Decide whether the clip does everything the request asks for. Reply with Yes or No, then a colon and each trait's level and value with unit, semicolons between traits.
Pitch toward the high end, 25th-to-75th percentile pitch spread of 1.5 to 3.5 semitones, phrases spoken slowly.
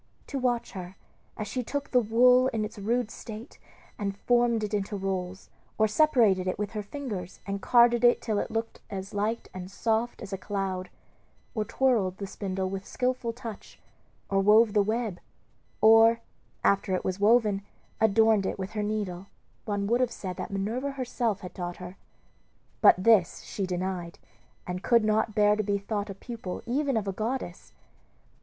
No: high, 210 Hz; average, 3.2 semitones; average, 175 wpm